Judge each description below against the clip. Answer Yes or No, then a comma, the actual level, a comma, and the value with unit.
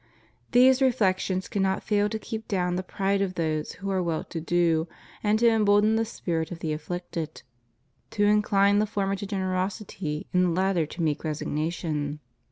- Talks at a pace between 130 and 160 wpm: No, average, 175 wpm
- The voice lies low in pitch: No, high, 190 Hz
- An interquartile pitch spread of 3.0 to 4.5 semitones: Yes, average, 3.8 semitones